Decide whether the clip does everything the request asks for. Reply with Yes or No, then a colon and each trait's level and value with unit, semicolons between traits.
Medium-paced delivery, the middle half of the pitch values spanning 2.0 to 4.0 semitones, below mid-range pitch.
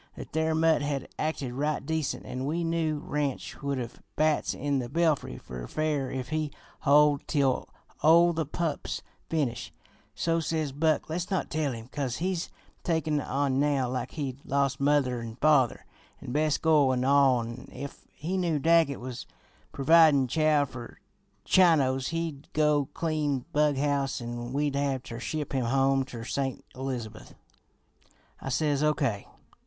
No: average, 160 wpm; average, 3.0 semitones; medium, 145 Hz